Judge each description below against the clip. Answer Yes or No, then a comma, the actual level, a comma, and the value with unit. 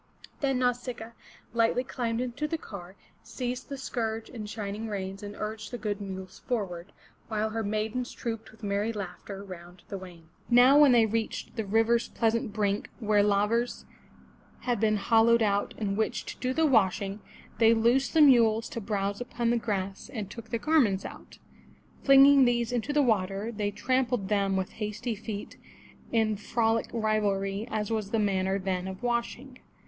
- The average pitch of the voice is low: No, high, 220 Hz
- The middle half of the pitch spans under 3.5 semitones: Yes, average, 3.0 semitones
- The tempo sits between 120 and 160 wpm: No, average, 175 wpm